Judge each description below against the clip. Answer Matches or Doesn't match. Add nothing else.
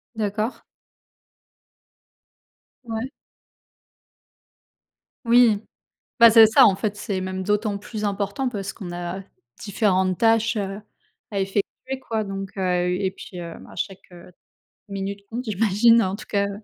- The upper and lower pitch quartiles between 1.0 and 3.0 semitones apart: Matches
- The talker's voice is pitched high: Matches